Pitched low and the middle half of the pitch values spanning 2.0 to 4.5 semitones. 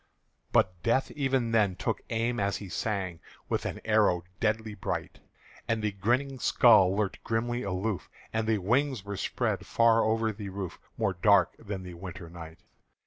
Yes: low, 105 Hz; average, 3.2 semitones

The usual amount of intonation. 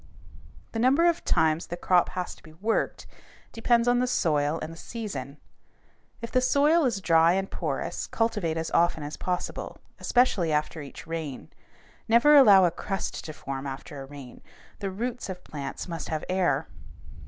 No: wide, 6.7 semitones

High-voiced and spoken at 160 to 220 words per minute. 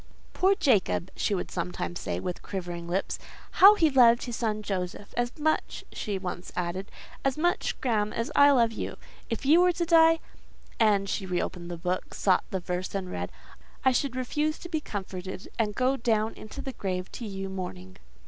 Yes: high, 210 Hz; average, 185 wpm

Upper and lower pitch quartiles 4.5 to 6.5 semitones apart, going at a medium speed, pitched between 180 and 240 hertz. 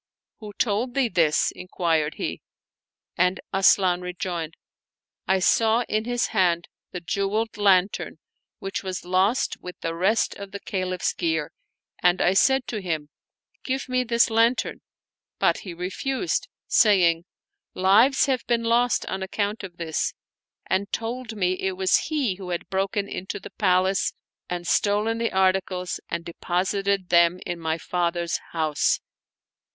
No: average, 3.7 semitones; average, 145 wpm; high, 190 Hz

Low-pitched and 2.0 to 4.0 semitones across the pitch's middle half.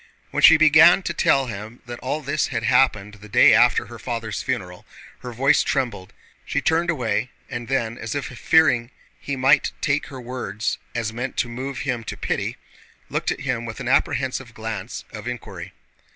Yes: low, 125 Hz; average, 3.3 semitones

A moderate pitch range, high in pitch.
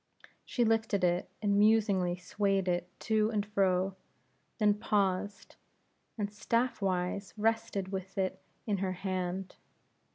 No: narrow, 2.3 semitones; high, 200 Hz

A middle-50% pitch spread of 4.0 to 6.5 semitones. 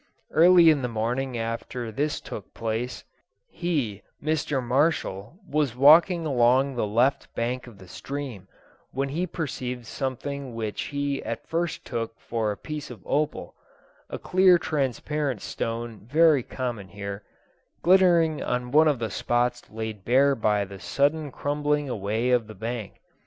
Yes: average, 4.6 semitones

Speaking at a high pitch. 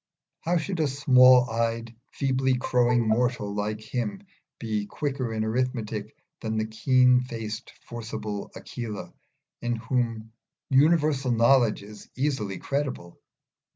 No: low, 120 Hz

